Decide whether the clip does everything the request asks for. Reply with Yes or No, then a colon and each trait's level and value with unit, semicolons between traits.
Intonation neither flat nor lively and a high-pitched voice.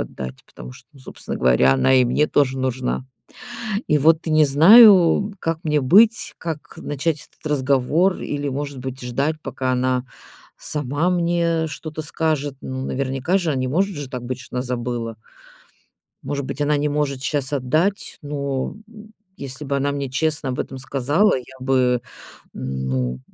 No: average, 3.4 semitones; medium, 140 Hz